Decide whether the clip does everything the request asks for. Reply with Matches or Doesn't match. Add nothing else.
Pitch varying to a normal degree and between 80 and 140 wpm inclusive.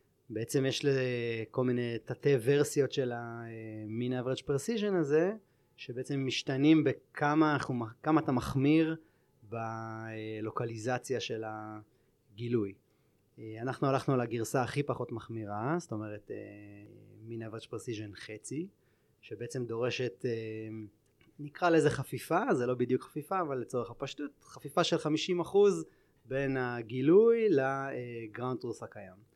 Matches